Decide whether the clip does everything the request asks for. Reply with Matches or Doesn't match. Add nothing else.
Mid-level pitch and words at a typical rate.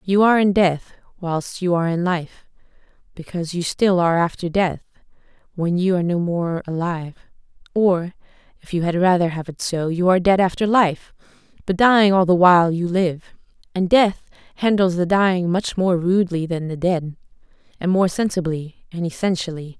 Matches